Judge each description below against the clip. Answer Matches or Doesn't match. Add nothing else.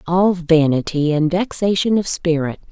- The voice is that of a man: Doesn't match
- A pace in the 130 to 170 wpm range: Matches